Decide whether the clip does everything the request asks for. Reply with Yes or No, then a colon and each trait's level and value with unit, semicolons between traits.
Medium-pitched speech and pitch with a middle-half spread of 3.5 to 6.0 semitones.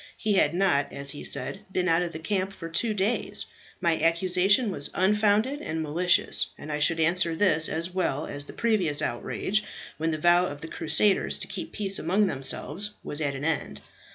Yes: medium, 175 Hz; average, 3.9 semitones